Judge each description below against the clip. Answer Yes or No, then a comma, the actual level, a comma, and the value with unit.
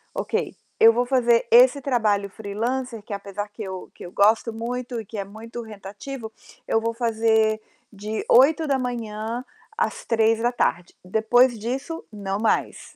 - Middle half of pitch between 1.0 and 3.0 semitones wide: Yes, narrow, 2.6 semitones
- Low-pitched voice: No, high, 225 Hz